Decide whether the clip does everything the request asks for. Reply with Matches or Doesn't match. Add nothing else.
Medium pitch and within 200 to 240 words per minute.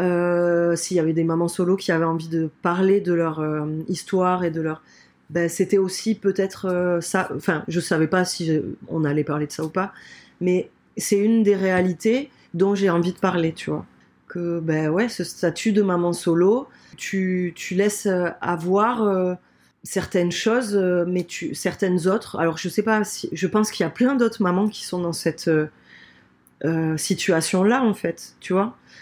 Doesn't match